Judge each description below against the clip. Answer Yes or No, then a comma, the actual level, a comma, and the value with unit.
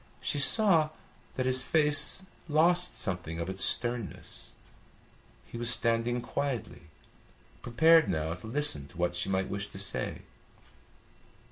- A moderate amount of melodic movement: No, wide, 7.7 semitones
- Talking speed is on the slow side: Yes, slow, 130 wpm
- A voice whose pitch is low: Yes, low, 120 Hz